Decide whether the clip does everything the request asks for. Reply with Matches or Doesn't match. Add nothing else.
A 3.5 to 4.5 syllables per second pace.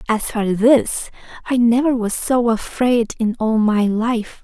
Matches